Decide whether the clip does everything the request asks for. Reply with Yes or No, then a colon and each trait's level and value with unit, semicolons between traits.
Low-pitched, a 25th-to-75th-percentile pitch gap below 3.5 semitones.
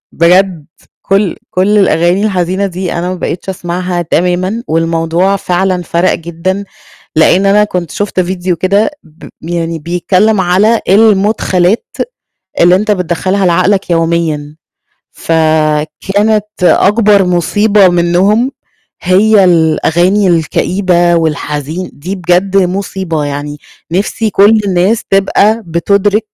No: medium, 180 Hz; average, 2.8 semitones